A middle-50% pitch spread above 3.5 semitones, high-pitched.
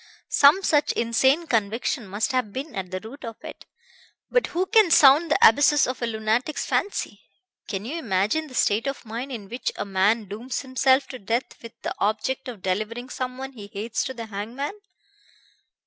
Yes: average, 4.1 semitones; high, 240 Hz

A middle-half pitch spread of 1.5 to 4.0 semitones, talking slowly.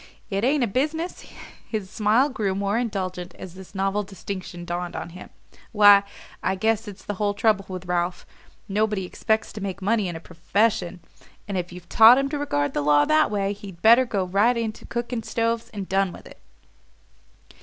No: average, 3.5 semitones; average, 185 wpm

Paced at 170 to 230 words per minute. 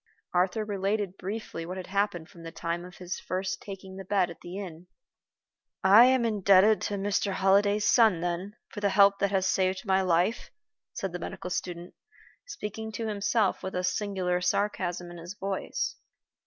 Yes: average, 175 wpm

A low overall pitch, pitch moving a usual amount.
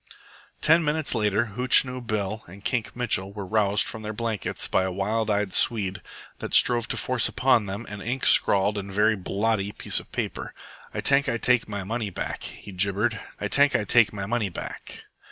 Yes: low, 110 Hz; average, 3.2 semitones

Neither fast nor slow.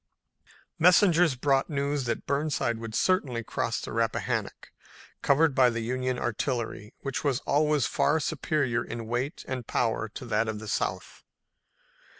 Yes: average, 145 wpm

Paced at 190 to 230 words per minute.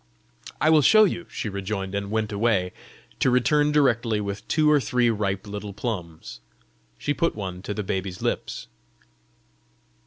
No: average, 155 wpm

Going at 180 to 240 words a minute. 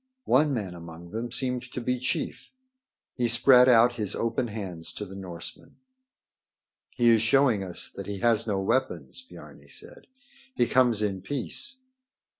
No: average, 155 wpm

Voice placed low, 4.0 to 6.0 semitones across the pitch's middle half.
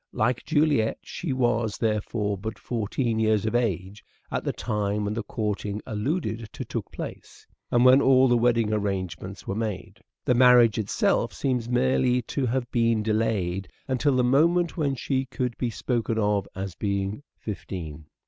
No: low, 115 Hz; average, 3.3 semitones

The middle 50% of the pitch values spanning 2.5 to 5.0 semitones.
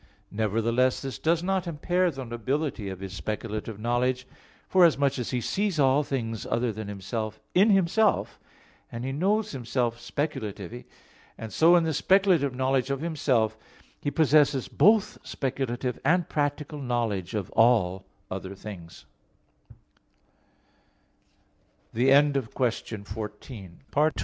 No: wide, 5.6 semitones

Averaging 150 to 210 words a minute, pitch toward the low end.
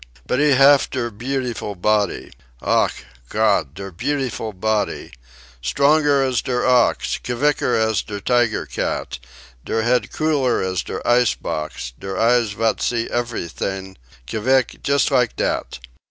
No: average, 140 wpm; low, 120 Hz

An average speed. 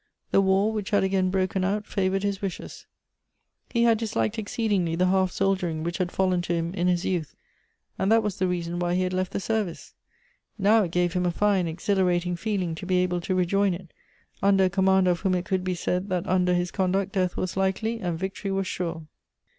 No: fast, 215 wpm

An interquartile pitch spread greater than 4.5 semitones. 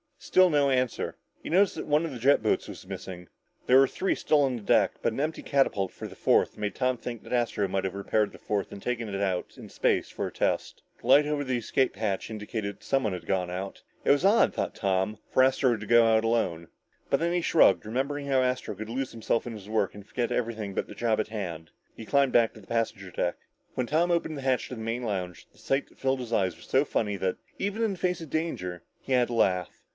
Yes: average, 5.2 semitones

